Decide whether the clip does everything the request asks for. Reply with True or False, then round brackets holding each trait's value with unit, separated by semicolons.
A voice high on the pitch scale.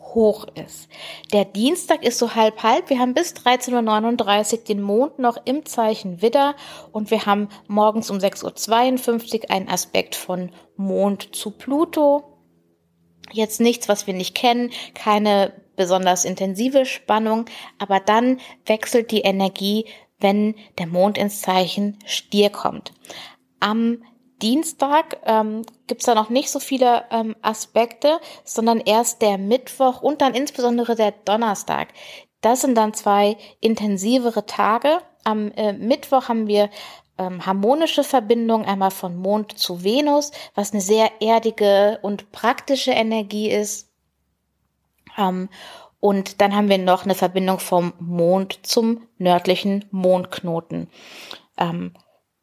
True (215 Hz)